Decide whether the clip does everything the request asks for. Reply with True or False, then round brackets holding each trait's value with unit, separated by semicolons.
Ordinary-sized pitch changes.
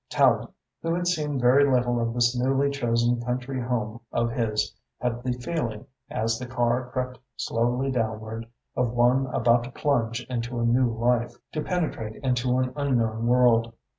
False (1.7 semitones)